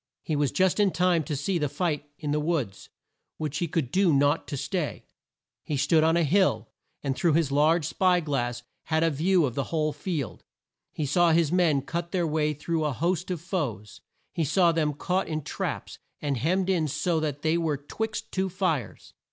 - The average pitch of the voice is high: No, medium, 160 Hz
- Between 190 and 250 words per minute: Yes, average, 200 wpm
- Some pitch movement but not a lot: Yes, average, 3.1 semitones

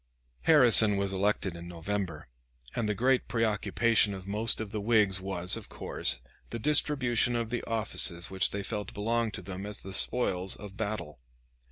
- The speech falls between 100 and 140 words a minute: No, average, 170 wpm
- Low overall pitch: Yes, low, 105 Hz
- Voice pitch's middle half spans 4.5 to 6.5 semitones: No, average, 3.1 semitones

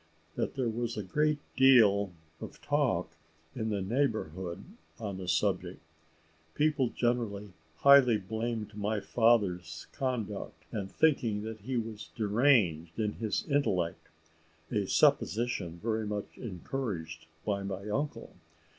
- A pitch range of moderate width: Yes, average, 3.8 semitones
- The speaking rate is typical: No, slow, 120 wpm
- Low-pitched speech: Yes, low, 110 Hz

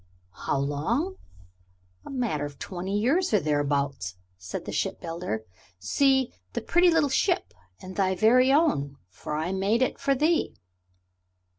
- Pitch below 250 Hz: Yes, high, 190 Hz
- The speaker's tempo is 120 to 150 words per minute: Yes, average, 145 wpm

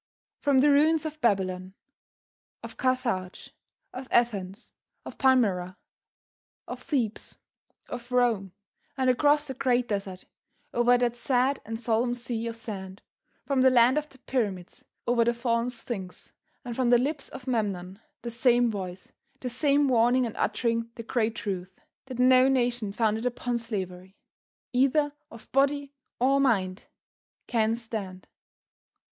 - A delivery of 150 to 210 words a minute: No, average, 140 wpm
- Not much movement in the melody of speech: No, average, 3.5 semitones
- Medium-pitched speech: No, high, 240 Hz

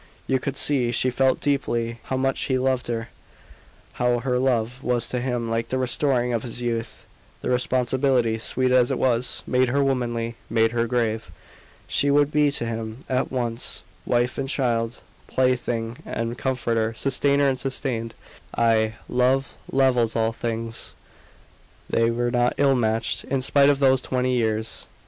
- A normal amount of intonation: No, narrow, 2.3 semitones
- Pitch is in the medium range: No, low, 125 Hz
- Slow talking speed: No, average, 160 wpm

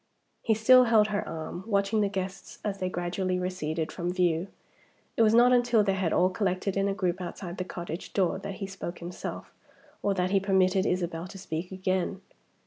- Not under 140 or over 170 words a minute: No, average, 195 wpm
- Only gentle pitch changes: Yes, narrow, 1.9 semitones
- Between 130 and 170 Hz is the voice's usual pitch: No, high, 190 Hz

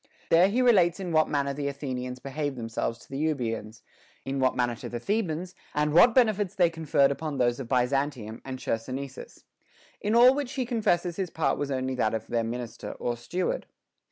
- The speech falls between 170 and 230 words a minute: Yes, average, 195 wpm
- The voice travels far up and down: Yes, wide, 5.8 semitones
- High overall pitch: No, medium, 140 Hz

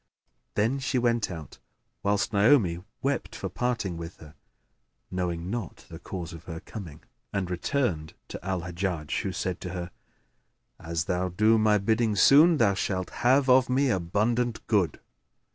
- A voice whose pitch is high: No, low, 100 Hz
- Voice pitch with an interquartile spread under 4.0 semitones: No, average, 5.2 semitones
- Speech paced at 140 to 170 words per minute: Yes, average, 155 wpm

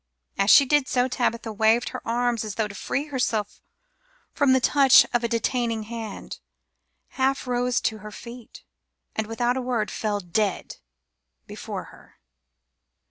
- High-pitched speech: Yes, high, 235 Hz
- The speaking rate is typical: Yes, average, 150 wpm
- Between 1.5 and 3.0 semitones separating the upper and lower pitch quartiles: Yes, narrow, 2.5 semitones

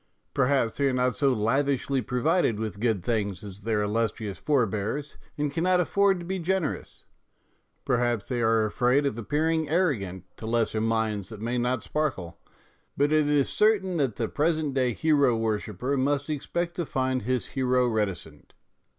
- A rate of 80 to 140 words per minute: No, average, 165 wpm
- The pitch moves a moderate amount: Yes, average, 5.0 semitones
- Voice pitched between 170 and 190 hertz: No, low, 125 Hz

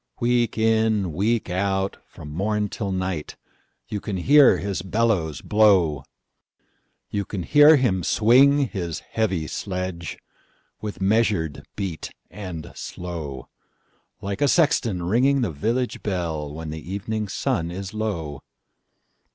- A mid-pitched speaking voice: No, low, 100 Hz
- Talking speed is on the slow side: Yes, slow, 110 wpm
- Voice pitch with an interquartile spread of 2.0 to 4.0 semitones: No, average, 4.5 semitones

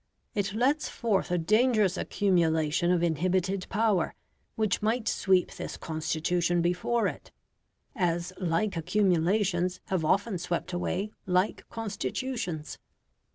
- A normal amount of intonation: Yes, average, 3.6 semitones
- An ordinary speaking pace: No, slow, 110 wpm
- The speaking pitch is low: No, medium, 185 Hz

